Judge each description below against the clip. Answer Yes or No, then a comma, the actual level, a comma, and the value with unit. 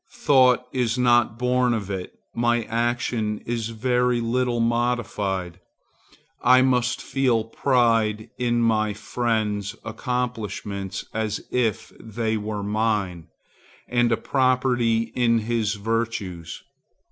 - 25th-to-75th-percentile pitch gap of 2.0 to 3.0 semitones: Yes, narrow, 2.4 semitones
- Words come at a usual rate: No, slow, 110 wpm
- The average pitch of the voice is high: No, low, 115 Hz